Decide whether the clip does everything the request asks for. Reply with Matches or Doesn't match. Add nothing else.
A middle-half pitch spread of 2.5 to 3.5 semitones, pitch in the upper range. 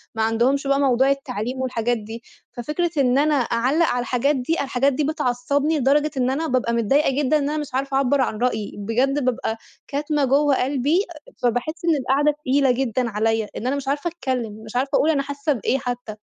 Matches